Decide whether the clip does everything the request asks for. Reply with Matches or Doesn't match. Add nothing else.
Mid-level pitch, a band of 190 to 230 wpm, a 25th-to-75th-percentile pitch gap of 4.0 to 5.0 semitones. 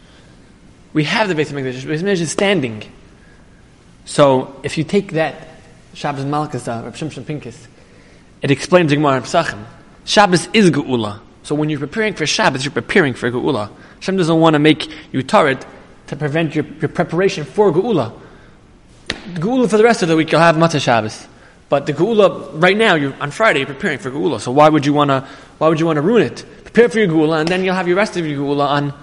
Matches